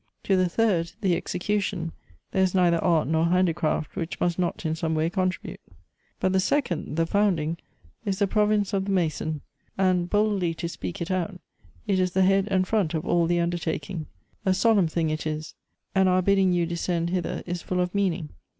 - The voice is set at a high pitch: No, medium, 180 Hz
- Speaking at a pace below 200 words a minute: No, fast, 205 wpm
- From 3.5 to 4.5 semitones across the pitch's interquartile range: No, narrow, 2.4 semitones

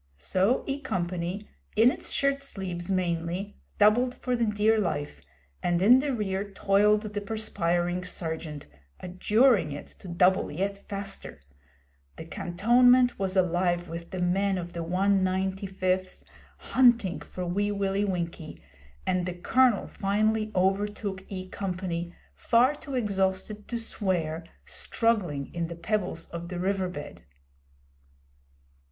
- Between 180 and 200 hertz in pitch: Yes, high, 190 Hz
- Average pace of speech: No, slow, 130 wpm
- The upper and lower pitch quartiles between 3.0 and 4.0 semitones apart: Yes, average, 3.3 semitones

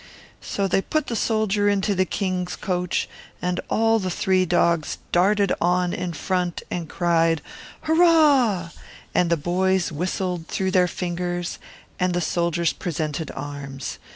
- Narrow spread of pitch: Yes, narrow, 2.1 semitones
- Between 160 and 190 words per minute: No, average, 140 wpm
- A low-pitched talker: No, medium, 180 Hz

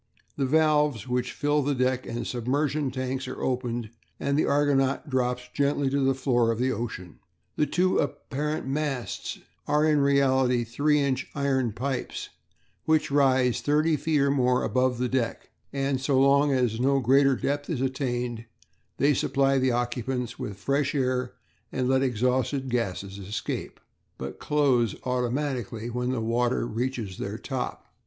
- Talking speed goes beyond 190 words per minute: No, average, 155 wpm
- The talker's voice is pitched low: Yes, low, 130 Hz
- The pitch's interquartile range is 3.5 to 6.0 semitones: No, narrow, 2.4 semitones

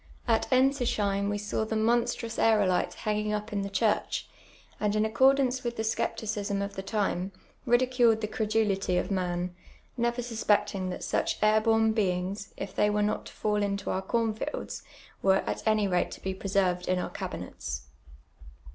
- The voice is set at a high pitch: Yes, high, 210 Hz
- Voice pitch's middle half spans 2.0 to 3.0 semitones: Yes, narrow, 2.4 semitones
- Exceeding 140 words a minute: Yes, average, 175 wpm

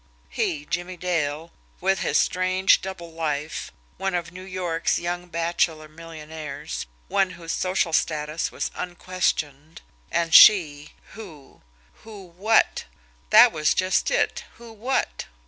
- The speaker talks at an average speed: No, slow, 125 wpm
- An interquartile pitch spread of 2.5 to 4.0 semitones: Yes, average, 2.9 semitones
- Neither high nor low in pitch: Yes, medium, 170 Hz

